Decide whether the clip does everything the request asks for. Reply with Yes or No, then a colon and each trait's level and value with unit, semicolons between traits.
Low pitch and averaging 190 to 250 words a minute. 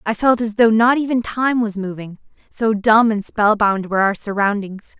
No: high, 215 Hz; fast, 205 wpm